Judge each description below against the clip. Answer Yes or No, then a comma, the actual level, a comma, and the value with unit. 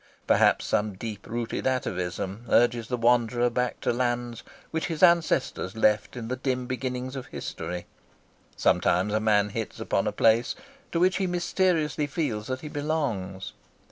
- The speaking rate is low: No, average, 155 wpm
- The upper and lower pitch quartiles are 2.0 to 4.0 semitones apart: No, average, 4.8 semitones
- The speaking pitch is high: No, low, 120 Hz